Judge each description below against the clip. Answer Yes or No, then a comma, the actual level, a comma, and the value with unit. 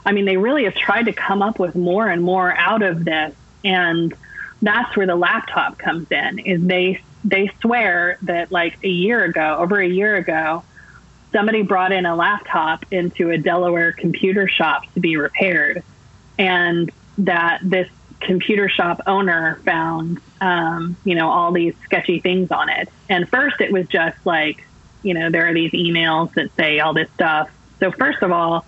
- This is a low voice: No, medium, 180 Hz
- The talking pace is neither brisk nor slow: Yes, average, 180 wpm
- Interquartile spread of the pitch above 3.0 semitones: No, narrow, 2.6 semitones